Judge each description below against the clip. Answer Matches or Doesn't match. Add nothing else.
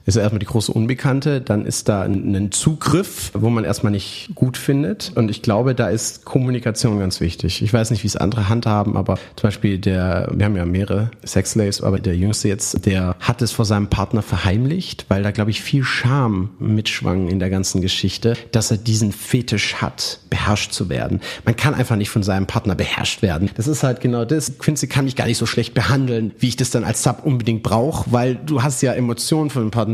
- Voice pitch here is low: Matches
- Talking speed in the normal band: Doesn't match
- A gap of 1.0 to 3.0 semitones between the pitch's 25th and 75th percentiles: Doesn't match